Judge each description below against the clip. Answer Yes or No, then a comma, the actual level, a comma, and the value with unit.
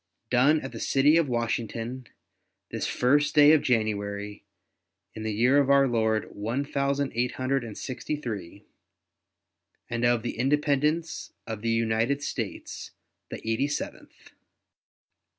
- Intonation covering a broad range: No, average, 4.0 semitones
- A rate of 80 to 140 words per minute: Yes, slow, 135 wpm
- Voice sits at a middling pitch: No, low, 125 Hz